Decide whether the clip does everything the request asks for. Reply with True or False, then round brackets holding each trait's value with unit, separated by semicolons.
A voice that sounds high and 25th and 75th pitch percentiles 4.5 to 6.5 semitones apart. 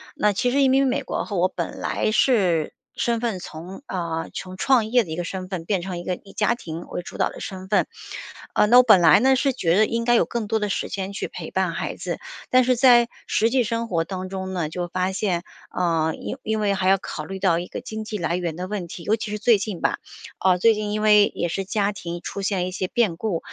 False (195 Hz; 3.8 semitones)